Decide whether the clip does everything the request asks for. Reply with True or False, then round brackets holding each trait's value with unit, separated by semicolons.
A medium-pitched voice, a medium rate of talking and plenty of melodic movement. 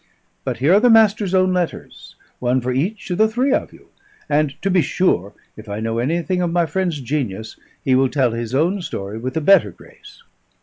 False (155 Hz; 210 wpm; 7.1 semitones)